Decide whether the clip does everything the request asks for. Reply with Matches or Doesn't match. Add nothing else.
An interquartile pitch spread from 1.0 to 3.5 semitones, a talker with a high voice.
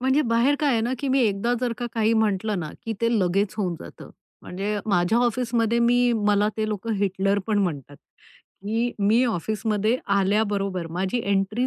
Matches